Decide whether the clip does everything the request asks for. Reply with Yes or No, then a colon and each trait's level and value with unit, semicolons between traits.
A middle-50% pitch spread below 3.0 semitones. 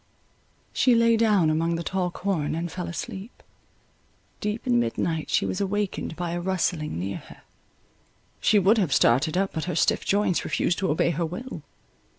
No: average, 3.9 semitones